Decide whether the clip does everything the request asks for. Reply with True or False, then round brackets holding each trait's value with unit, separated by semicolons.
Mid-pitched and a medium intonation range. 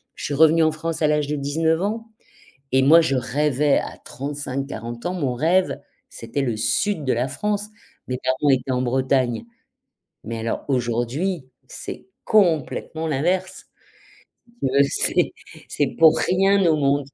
True (145 Hz; 4.1 semitones)